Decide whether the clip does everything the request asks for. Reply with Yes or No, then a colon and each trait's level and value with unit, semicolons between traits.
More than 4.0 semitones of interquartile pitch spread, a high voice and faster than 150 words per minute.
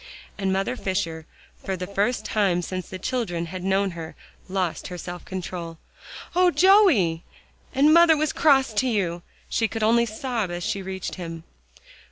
Yes: average, 5.1 semitones; high, 195 Hz; average, 165 wpm